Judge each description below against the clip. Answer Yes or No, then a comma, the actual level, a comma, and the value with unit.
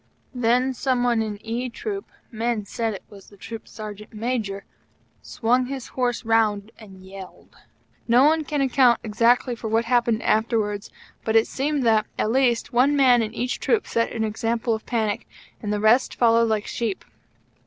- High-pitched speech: Yes, high, 230 Hz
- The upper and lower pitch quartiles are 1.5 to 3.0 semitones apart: Yes, narrow, 2.4 semitones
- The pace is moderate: Yes, average, 175 wpm